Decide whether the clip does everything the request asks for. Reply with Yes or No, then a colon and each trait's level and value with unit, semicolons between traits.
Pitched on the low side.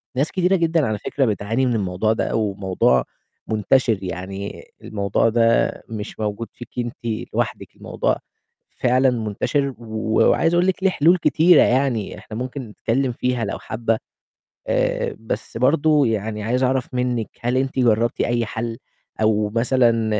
Yes: low, 115 Hz